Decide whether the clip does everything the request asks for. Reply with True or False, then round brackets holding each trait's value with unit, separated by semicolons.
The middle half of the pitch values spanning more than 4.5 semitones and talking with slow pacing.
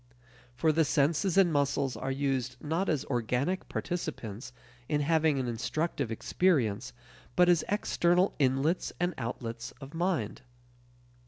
True (5.1 semitones; 130 wpm)